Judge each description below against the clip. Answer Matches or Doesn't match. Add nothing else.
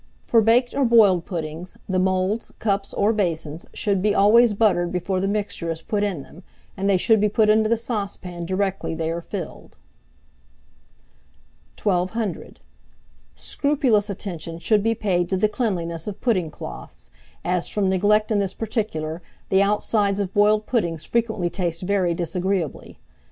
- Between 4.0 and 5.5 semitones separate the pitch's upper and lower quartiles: Doesn't match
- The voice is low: Doesn't match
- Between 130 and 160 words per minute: Matches